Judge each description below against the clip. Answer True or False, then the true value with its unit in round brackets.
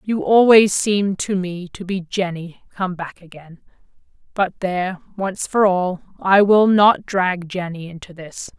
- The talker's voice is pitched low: False (185 Hz)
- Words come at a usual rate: True (160 wpm)